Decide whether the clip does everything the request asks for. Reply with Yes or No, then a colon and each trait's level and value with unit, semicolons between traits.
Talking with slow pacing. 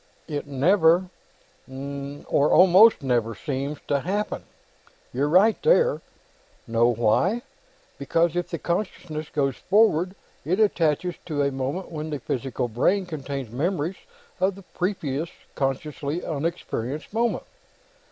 Yes: slow, 120 wpm